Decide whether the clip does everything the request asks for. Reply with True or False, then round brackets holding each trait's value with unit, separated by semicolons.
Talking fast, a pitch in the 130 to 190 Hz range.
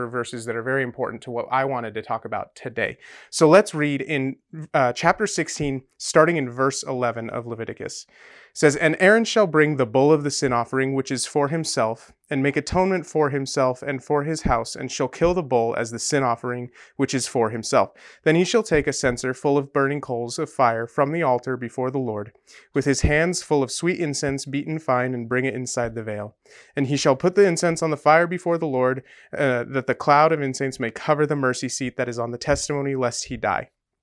True (225 wpm; 135 Hz)